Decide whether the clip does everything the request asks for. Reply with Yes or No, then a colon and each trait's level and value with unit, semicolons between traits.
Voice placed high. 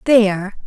Yes: high, 210 Hz